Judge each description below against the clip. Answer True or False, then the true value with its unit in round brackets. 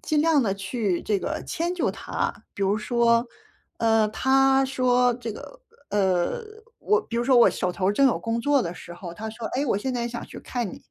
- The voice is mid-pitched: False (235 Hz)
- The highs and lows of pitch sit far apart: False (4.4 semitones)